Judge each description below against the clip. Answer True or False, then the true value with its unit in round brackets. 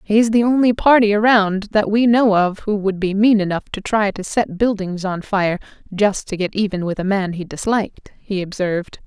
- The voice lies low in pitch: False (205 Hz)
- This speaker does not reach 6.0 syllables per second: True (5.0 syllables/s)